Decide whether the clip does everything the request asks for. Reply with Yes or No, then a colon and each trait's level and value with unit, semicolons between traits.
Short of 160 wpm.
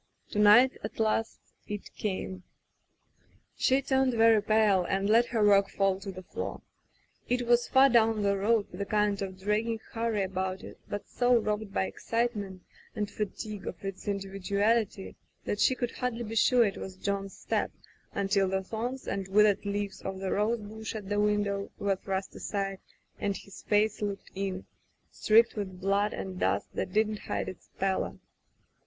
No: average, 175 wpm